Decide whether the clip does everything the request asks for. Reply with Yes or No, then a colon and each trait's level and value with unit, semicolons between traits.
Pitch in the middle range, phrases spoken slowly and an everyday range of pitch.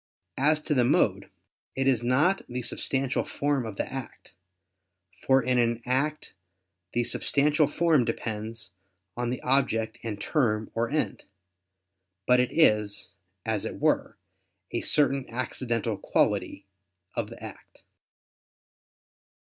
No: low, 125 Hz; slow, 125 wpm; average, 3.3 semitones